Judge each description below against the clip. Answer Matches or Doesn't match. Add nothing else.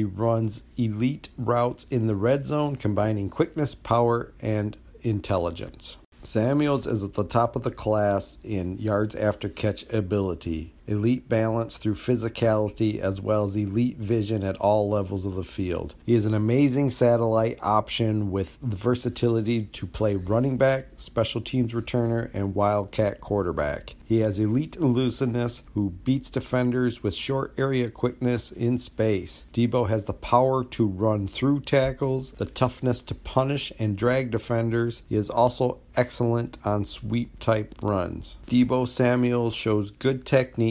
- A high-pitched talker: Doesn't match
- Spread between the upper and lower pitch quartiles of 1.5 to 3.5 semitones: Matches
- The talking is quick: Doesn't match